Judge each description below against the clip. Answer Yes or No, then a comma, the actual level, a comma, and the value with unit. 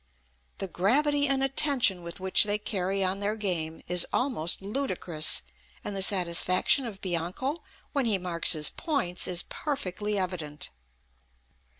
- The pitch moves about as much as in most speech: No, wide, 5.9 semitones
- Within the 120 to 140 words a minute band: Yes, slow, 135 wpm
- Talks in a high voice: Yes, high, 195 Hz